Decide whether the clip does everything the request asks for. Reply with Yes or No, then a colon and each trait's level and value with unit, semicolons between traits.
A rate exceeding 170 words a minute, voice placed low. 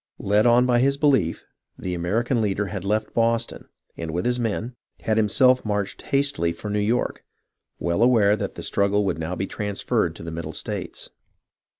Yes: average, 180 wpm; low, 105 Hz